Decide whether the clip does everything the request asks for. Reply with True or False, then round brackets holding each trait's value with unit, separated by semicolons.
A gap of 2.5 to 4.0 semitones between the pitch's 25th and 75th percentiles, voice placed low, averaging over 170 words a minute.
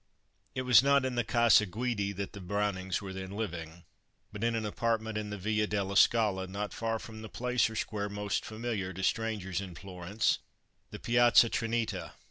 True (2.9 semitones; 105 Hz; 185 wpm)